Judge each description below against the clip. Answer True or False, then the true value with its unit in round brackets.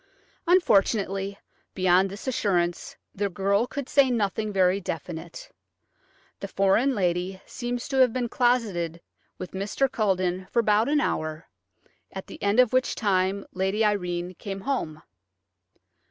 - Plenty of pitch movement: False (4.3 semitones)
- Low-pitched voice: False (195 Hz)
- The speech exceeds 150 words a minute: False (135 wpm)